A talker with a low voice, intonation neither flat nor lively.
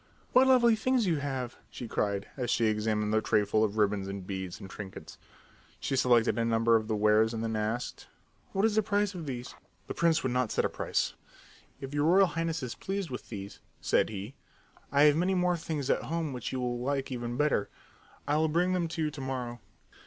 No: low, 125 Hz; wide, 6.9 semitones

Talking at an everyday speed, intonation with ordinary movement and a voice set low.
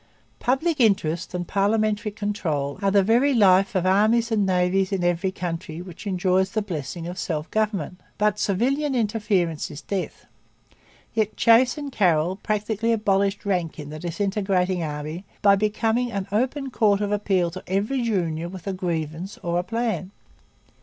No: average, 160 wpm; average, 3.4 semitones; high, 195 Hz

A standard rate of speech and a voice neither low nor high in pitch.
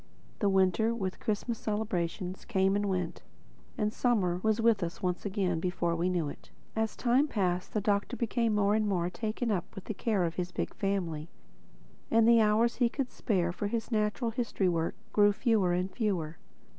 No: average, 185 wpm; high, 205 Hz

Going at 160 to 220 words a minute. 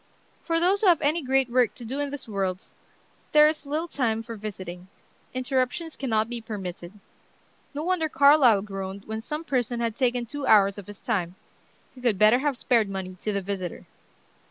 Yes: average, 185 wpm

